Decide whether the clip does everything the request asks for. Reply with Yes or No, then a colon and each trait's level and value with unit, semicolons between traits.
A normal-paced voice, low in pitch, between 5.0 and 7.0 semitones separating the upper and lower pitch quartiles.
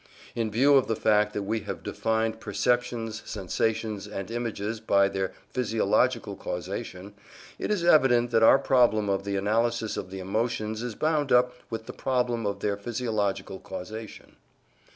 No: average, 155 wpm; low, 110 Hz; average, 3.0 semitones